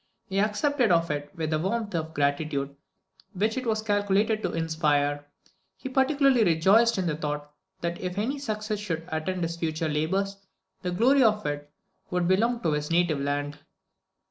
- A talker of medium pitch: Yes, medium, 175 Hz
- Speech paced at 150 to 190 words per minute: Yes, average, 170 wpm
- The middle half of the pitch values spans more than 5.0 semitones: Yes, wide, 5.6 semitones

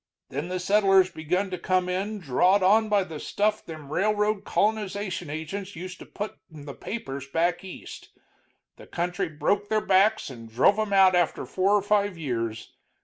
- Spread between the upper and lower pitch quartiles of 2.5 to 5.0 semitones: Yes, average, 4.1 semitones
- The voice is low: No, medium, 185 Hz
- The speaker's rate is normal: Yes, average, 175 wpm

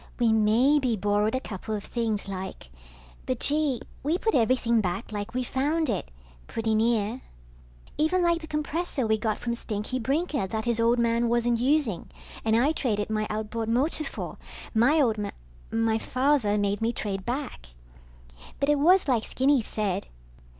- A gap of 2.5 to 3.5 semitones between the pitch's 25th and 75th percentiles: No, average, 4.4 semitones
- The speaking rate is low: No, average, 165 wpm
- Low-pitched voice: No, high, 235 Hz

